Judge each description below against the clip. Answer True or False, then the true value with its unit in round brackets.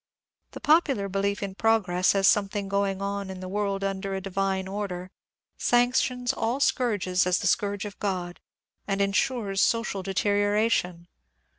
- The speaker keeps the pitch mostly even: True (1.5 semitones)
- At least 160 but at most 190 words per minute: False (150 wpm)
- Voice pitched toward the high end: True (200 Hz)